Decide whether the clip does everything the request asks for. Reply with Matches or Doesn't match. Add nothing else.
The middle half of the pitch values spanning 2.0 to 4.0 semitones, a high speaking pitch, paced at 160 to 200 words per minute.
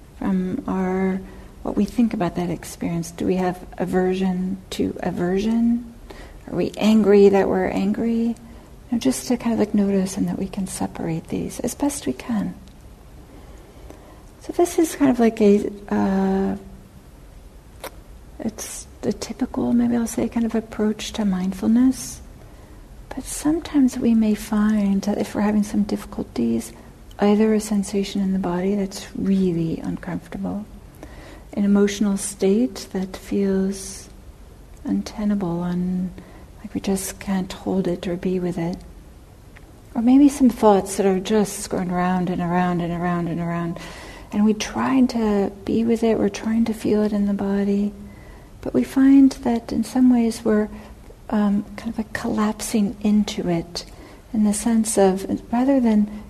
Doesn't match